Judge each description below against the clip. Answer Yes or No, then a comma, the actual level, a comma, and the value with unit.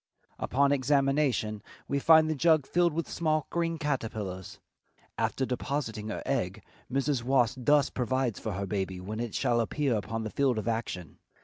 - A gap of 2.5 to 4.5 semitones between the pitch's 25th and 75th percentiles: No, average, 5.0 semitones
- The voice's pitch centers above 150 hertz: No, low, 130 Hz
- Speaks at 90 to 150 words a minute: No, average, 165 wpm